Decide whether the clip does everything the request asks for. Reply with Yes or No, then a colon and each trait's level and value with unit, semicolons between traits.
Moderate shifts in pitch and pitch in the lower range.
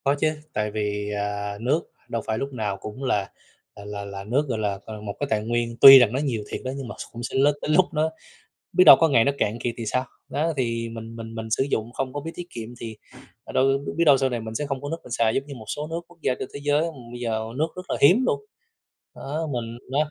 Yes: average, 4.5 semitones; low, 120 Hz